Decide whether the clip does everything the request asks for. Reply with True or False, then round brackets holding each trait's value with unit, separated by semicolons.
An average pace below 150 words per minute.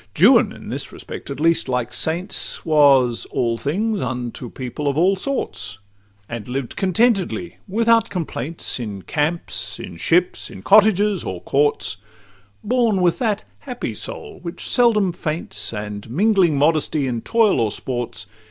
True (140 wpm)